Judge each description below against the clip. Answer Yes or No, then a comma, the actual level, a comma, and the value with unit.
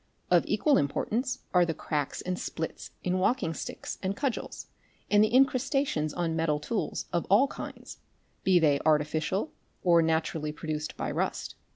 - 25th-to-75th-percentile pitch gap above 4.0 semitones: Yes, wide, 5.6 semitones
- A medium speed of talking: Yes, average, 155 wpm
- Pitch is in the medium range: Yes, medium, 175 Hz